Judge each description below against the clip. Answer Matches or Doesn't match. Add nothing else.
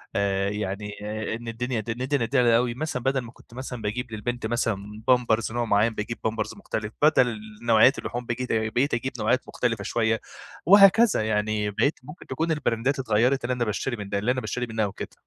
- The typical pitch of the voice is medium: Doesn't match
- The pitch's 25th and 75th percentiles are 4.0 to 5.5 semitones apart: Doesn't match